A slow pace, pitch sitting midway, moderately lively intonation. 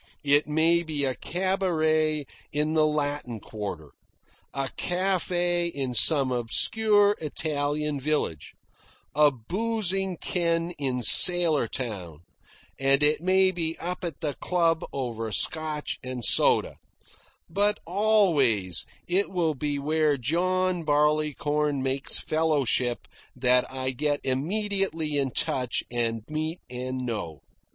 Yes: slow, 115 wpm; medium, 150 Hz; average, 4.8 semitones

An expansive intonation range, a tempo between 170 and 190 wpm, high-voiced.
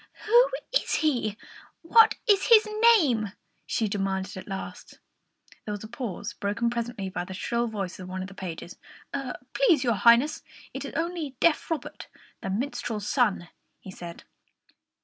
No: wide, 7.3 semitones; average, 155 wpm; high, 225 Hz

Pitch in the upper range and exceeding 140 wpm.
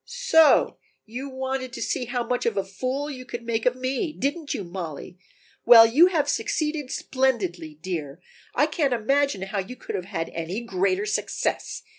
Yes: high, 245 Hz; average, 175 wpm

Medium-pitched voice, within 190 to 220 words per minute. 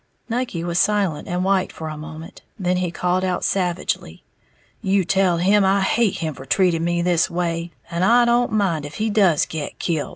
Yes: medium, 180 Hz; average, 195 wpm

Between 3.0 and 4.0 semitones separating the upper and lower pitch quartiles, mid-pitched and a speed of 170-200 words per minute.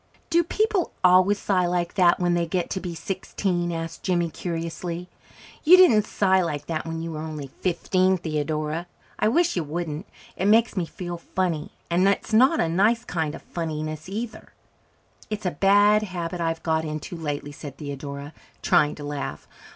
Yes: average, 3.5 semitones; medium, 175 Hz; average, 175 wpm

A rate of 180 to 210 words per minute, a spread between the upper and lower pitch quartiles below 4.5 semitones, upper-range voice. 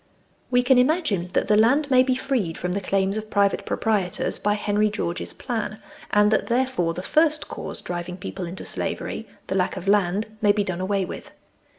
No: average, 195 wpm; average, 4.8 semitones; high, 210 Hz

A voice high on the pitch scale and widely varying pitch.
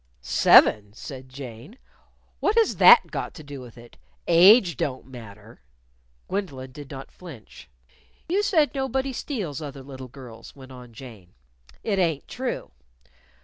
No: low, 135 Hz; wide, 7.9 semitones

